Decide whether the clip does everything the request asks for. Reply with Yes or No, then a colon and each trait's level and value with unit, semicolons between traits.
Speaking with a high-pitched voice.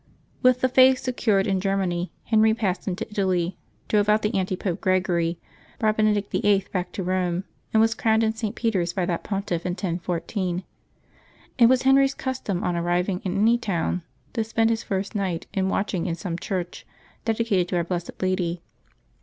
Yes: high, 195 Hz